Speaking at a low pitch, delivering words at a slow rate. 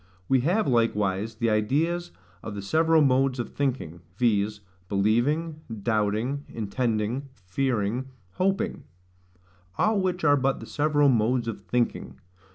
Yes: low, 125 Hz; slow, 125 wpm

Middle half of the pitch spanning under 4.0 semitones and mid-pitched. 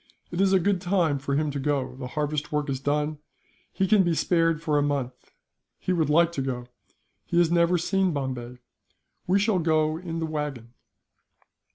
Yes: average, 3.6 semitones; medium, 155 Hz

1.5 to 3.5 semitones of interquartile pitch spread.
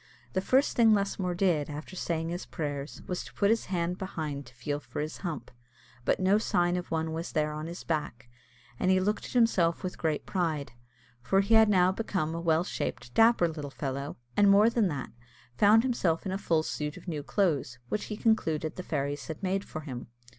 No: average, 4.5 semitones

